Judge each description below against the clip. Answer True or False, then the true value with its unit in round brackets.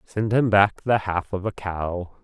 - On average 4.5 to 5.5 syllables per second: False (3.9 syllables/s)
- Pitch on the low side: True (100 Hz)